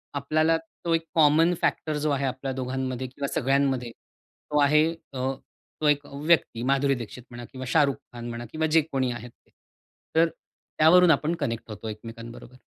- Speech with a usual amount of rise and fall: Yes, average, 3.7 semitones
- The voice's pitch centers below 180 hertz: Yes, medium, 140 Hz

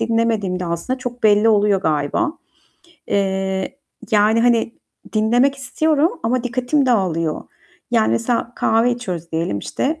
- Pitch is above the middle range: Yes, high, 220 Hz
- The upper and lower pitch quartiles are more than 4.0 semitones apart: Yes, average, 4.6 semitones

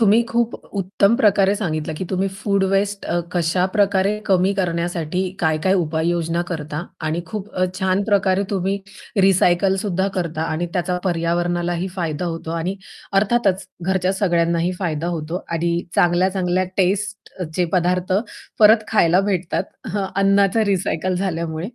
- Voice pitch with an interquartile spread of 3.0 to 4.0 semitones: No, narrow, 2.5 semitones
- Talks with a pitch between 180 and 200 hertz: Yes, medium, 185 Hz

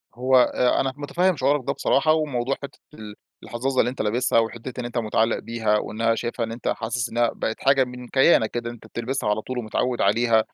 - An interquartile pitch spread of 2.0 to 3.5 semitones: Yes, narrow, 2.6 semitones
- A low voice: Yes, low, 120 Hz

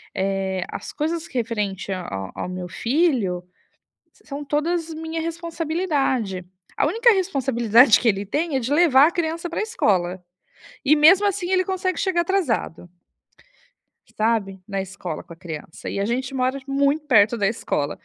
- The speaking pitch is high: Yes, very high, 265 Hz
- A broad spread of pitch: Yes, wide, 9.0 semitones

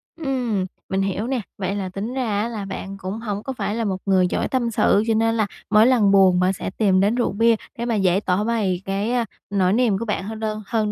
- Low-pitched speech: No, high, 210 Hz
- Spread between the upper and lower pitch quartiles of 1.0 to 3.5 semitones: Yes, average, 3.0 semitones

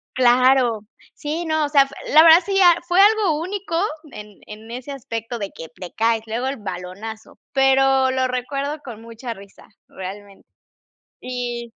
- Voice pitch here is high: Yes, very high, 255 Hz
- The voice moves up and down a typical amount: Yes, average, 4.6 semitones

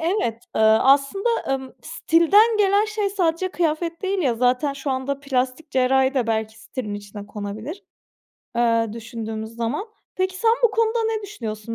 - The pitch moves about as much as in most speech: No, wide, 8.6 semitones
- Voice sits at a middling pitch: No, very high, 275 Hz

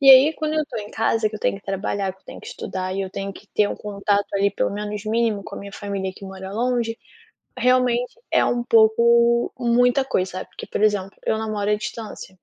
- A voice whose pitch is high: Yes, high, 215 Hz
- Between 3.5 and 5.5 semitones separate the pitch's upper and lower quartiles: No, average, 3.1 semitones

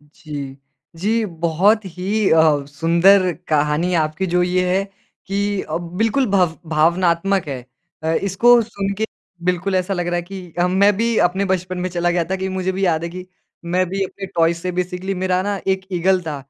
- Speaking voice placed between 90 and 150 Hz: No, medium, 180 Hz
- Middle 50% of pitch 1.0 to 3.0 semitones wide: Yes, narrow, 2.5 semitones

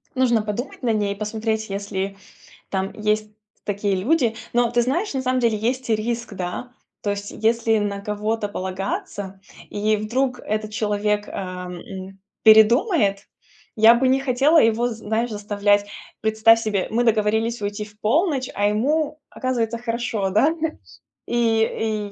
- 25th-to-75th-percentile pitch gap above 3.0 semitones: No, average, 2.7 semitones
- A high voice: Yes, high, 220 Hz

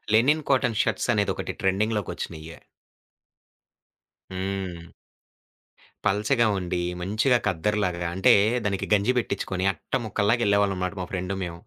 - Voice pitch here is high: No, low, 100 Hz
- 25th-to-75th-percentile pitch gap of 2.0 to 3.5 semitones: Yes, average, 2.8 semitones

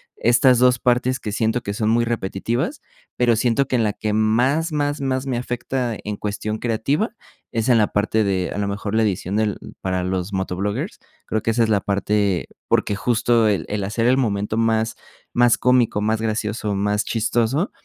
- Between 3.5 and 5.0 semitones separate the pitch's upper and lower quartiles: No, average, 3.0 semitones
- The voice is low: Yes, low, 110 Hz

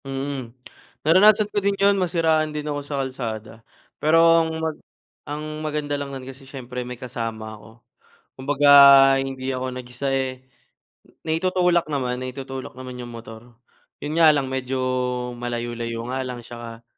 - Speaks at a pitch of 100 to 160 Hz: Yes, low, 135 Hz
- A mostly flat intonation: No, average, 3.7 semitones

